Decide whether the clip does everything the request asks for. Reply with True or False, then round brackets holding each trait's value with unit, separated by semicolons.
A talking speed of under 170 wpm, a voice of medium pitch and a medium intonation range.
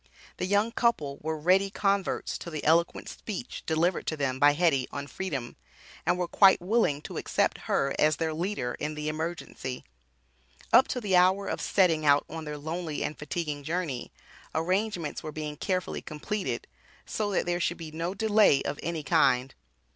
False (175 wpm; 165 Hz; 3.9 semitones)